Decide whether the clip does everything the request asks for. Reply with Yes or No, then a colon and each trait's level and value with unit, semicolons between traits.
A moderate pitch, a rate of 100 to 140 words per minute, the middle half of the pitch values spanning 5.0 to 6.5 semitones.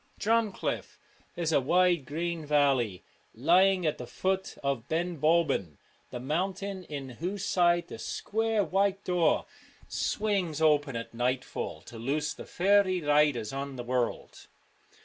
Yes: medium, 160 Hz; slow, 135 wpm; wide, 5.5 semitones